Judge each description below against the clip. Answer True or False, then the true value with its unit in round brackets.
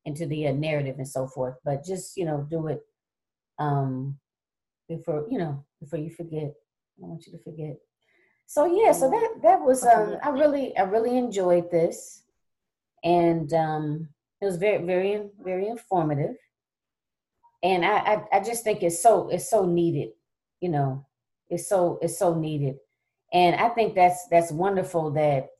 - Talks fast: False (170 wpm)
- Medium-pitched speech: True (170 Hz)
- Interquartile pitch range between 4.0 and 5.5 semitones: True (4.7 semitones)